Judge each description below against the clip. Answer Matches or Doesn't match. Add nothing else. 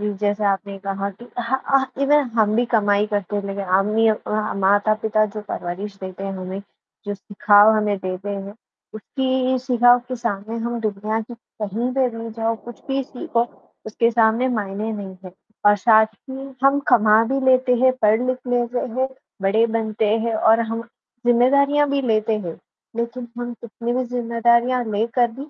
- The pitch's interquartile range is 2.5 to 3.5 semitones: Matches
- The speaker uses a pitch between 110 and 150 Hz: Doesn't match